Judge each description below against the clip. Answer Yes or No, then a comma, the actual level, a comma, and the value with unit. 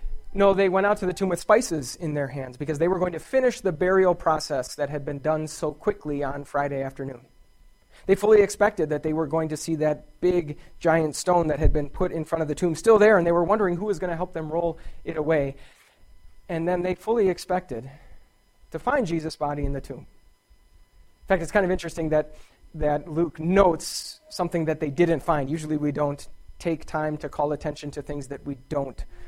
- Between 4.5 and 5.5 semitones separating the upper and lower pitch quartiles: No, average, 3.8 semitones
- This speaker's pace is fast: Yes, fast, 220 wpm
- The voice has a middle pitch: Yes, medium, 160 Hz